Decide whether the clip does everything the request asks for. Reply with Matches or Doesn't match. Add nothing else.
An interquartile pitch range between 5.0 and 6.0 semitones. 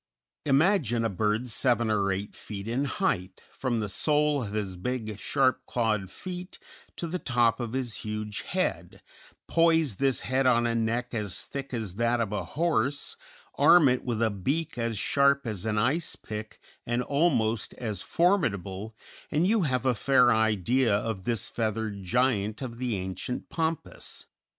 Doesn't match